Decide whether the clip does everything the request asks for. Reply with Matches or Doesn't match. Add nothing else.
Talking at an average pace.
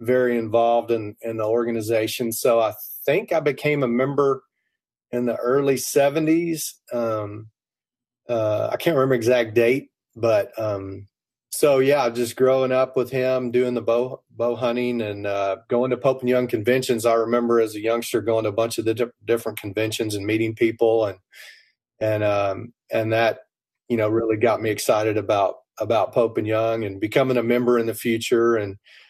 Matches